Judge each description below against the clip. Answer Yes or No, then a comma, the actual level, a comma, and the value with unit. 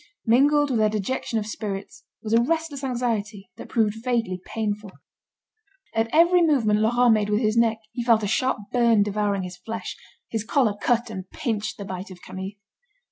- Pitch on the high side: Yes, high, 225 Hz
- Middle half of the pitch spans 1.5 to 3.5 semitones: Yes, average, 2.9 semitones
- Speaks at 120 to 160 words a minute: No, average, 180 wpm